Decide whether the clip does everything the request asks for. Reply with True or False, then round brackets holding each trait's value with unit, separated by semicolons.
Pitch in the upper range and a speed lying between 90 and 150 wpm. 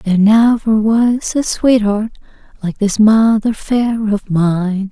True (215 Hz; 135 wpm)